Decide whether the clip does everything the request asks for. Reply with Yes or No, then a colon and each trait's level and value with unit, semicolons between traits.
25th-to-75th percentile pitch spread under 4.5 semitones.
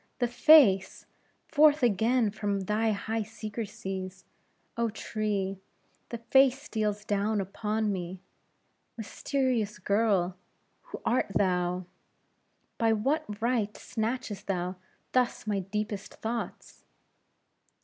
Yes: average, 3.1 semitones